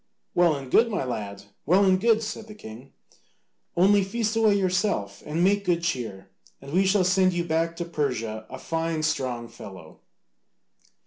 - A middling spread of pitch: No, wide, 7.4 semitones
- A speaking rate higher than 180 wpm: No, average, 170 wpm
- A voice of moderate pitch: Yes, medium, 170 Hz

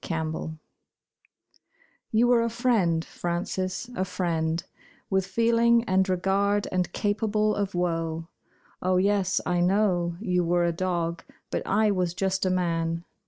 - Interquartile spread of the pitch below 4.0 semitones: Yes, average, 3.0 semitones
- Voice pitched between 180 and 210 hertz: Yes, medium, 185 Hz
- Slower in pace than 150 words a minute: Yes, slow, 135 wpm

